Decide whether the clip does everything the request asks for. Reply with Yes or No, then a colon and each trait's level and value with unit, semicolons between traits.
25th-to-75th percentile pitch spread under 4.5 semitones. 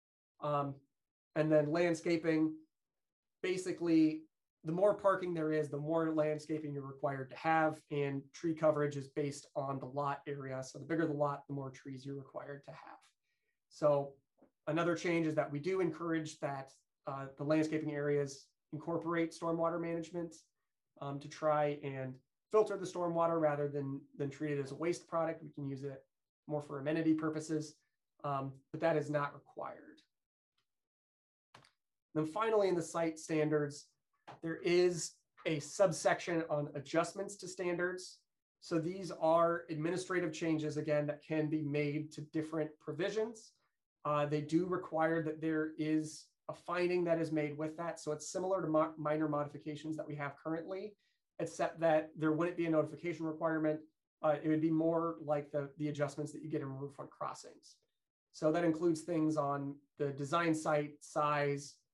Yes: narrow, 2.4 semitones